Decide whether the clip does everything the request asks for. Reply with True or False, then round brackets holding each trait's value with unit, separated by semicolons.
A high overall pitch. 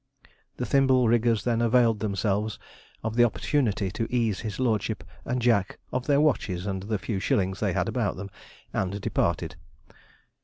False (110 Hz)